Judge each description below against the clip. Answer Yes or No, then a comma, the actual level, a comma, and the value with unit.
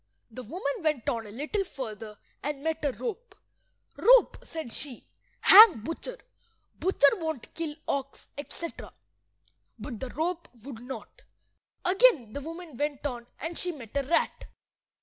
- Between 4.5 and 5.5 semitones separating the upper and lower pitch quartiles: Yes, average, 5.2 semitones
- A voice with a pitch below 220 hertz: No, very high, 295 Hz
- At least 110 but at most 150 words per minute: Yes, average, 145 wpm